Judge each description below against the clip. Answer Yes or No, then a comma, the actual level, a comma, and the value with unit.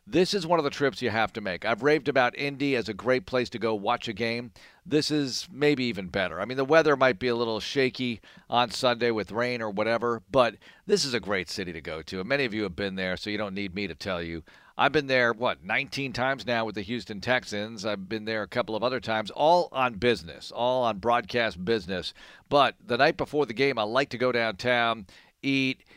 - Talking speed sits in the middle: No, fast, 245 wpm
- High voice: No, low, 120 Hz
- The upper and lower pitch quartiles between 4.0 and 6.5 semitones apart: No, average, 3.6 semitones